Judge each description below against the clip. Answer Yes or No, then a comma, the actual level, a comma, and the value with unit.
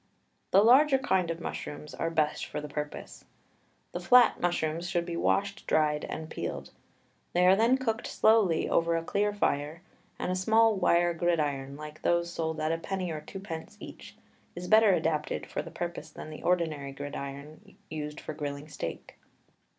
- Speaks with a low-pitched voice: No, medium, 165 Hz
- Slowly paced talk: No, average, 170 wpm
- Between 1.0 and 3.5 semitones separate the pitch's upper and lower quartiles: No, average, 3.9 semitones